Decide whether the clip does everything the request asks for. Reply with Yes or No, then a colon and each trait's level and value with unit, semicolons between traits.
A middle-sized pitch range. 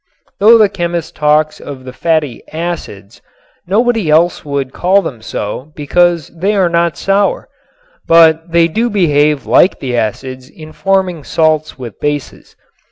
Yes: average, 3.6 semitones